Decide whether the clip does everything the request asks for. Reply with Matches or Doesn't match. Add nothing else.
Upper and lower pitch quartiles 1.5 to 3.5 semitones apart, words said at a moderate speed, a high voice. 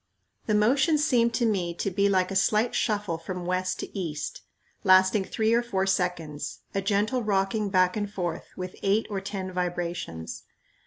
Matches